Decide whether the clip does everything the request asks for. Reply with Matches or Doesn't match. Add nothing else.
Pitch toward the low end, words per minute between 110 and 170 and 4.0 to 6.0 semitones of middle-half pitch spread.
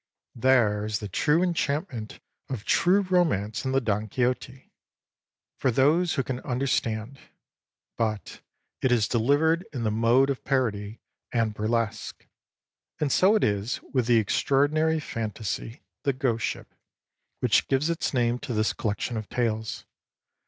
Matches